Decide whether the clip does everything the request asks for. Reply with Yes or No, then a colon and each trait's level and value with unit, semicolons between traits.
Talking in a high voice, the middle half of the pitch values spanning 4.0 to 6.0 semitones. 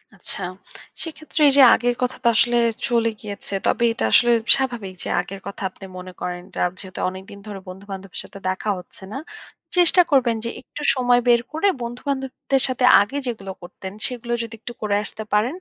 Yes: high, 235 Hz; average, 4.4 semitones